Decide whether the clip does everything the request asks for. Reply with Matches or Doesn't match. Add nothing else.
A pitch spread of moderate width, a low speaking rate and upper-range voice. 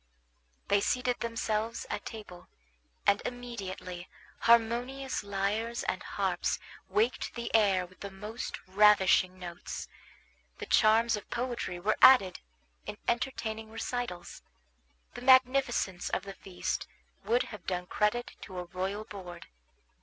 Matches